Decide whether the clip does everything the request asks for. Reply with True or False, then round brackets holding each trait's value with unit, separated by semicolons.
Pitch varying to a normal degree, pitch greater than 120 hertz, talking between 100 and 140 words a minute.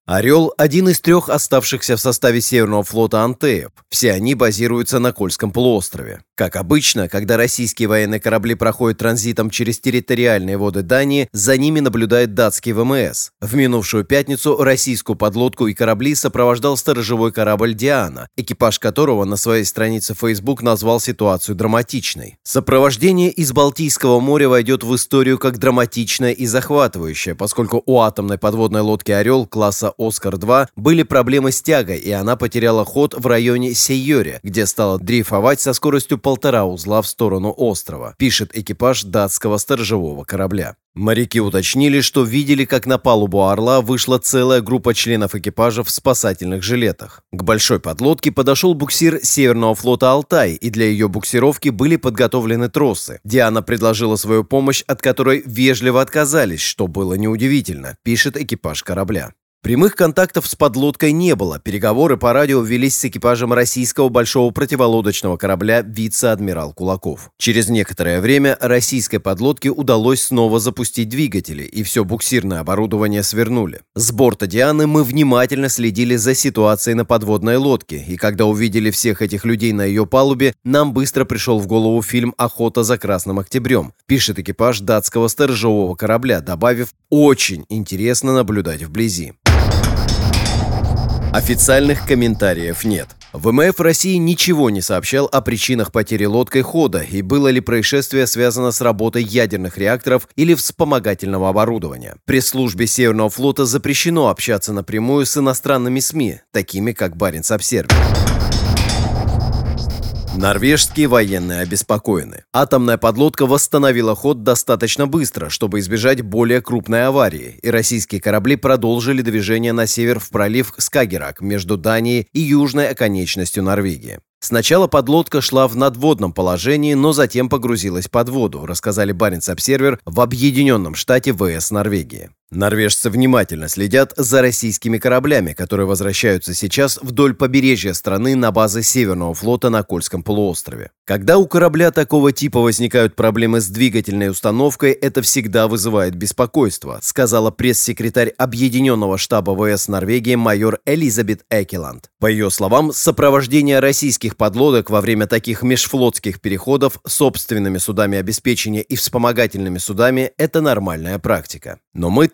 False (4.0 semitones; 115 Hz; 135 wpm)